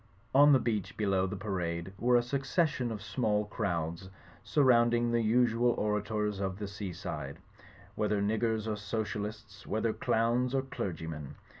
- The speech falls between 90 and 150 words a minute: Yes, average, 140 wpm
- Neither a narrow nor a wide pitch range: Yes, average, 3.2 semitones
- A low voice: Yes, low, 110 Hz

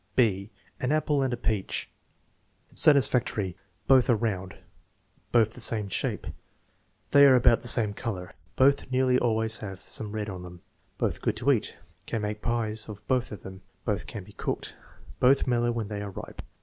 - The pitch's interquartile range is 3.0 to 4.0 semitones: Yes, average, 3.6 semitones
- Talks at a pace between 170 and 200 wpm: Yes, average, 175 wpm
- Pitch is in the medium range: No, low, 110 Hz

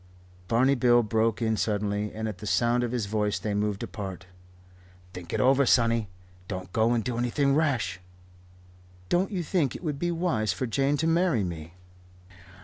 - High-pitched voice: No, low, 115 Hz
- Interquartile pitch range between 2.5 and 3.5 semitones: No, average, 4.8 semitones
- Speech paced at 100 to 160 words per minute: No, average, 175 wpm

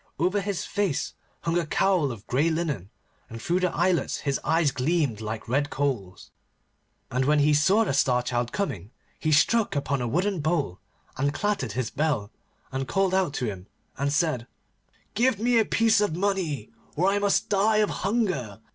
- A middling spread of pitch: No, wide, 7.1 semitones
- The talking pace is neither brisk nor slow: Yes, average, 180 wpm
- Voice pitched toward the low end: No, medium, 155 Hz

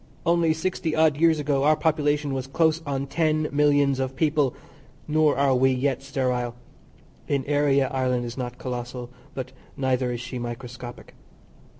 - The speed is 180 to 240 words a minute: No, average, 155 wpm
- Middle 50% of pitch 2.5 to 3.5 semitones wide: Yes, average, 2.9 semitones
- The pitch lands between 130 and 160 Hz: Yes, low, 135 Hz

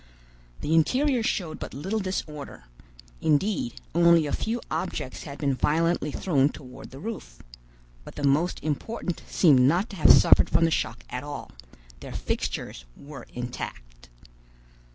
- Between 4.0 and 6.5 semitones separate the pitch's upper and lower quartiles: Yes, average, 4.7 semitones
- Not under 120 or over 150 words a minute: Yes, average, 145 wpm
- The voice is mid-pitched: Yes, medium, 155 Hz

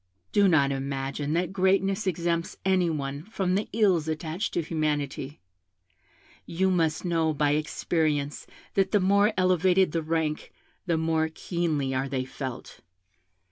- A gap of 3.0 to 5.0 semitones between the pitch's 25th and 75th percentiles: Yes, average, 3.9 semitones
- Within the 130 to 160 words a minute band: Yes, average, 140 wpm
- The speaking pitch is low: No, medium, 165 Hz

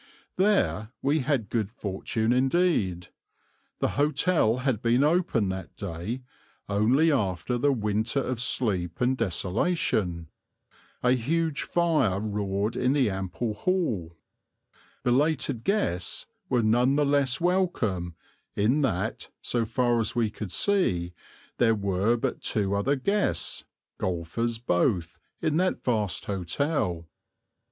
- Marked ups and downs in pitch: Yes, wide, 6.1 semitones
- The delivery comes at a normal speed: No, slow, 120 wpm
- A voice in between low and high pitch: No, low, 115 Hz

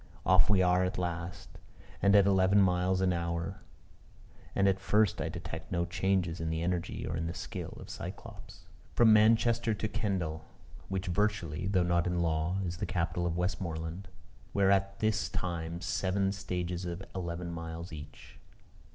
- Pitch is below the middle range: Yes, very low, 90 Hz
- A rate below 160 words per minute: No, average, 165 wpm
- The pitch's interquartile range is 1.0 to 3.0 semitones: Yes, narrow, 2.4 semitones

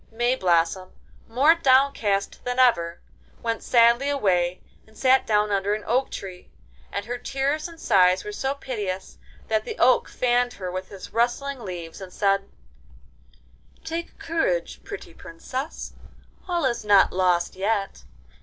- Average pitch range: No, wide, 5.8 semitones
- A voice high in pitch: Yes, high, 230 Hz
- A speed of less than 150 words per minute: Yes, average, 140 wpm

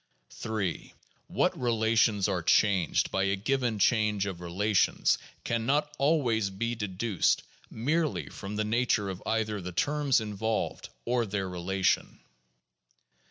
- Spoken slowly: Yes, slow, 125 wpm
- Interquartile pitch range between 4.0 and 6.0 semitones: No, average, 3.4 semitones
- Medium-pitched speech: No, low, 105 Hz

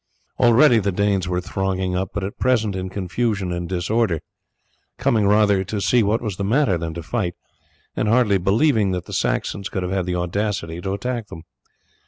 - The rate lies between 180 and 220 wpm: Yes, average, 190 wpm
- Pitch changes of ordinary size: Yes, average, 3.3 semitones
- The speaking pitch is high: No, low, 100 Hz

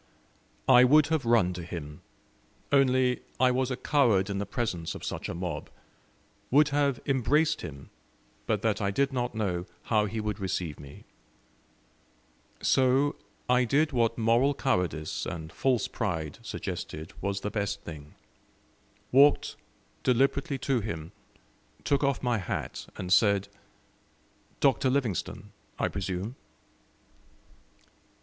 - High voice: No, low, 115 Hz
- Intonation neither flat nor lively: No, wide, 6.4 semitones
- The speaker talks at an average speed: No, slow, 130 wpm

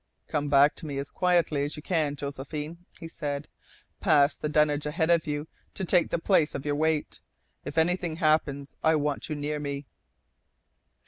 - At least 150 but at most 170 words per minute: No, average, 180 wpm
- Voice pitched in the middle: Yes, medium, 150 Hz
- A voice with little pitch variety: Yes, narrow, 1.9 semitones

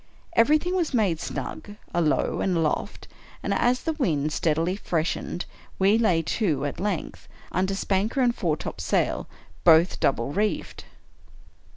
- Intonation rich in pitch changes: Yes, wide, 5.7 semitones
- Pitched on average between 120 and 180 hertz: No, high, 190 Hz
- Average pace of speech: No, slow, 130 wpm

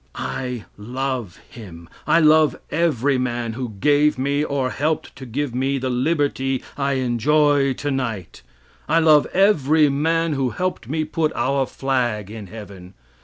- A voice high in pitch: No, low, 135 Hz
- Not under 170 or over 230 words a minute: No, average, 145 wpm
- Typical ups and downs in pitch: Yes, average, 3.6 semitones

